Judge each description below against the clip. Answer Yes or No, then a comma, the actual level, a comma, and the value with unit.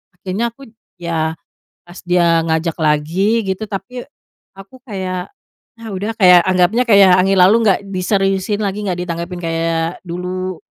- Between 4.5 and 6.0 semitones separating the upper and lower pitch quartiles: No, narrow, 2.6 semitones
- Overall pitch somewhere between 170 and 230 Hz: Yes, medium, 185 Hz